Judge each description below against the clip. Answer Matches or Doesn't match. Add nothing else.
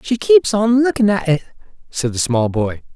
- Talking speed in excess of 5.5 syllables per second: Doesn't match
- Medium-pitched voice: Matches